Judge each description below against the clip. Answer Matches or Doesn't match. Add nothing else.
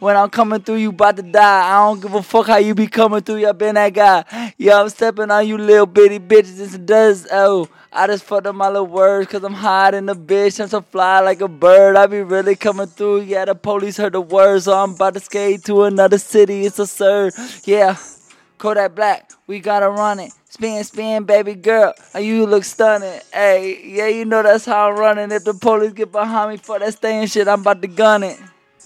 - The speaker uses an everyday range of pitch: Doesn't match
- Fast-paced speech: Matches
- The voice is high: Matches